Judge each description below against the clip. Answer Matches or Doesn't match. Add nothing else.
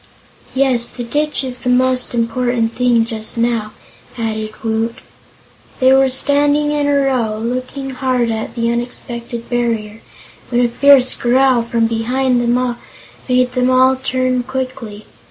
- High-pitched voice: Matches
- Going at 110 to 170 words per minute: Matches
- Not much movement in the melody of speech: Matches